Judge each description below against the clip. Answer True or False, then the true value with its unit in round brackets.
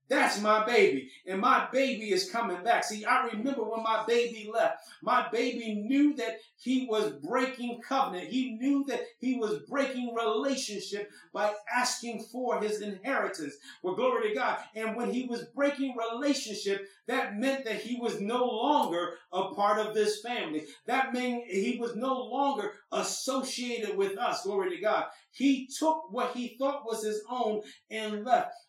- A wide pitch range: False (3.5 semitones)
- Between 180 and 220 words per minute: False (165 wpm)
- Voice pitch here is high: True (235 Hz)